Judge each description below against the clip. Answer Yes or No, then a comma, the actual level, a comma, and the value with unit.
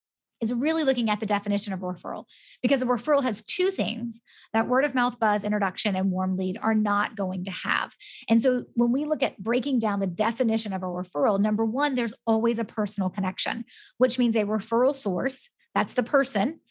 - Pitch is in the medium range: No, high, 225 Hz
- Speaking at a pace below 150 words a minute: No, fast, 205 wpm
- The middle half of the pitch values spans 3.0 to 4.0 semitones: Yes, average, 3.7 semitones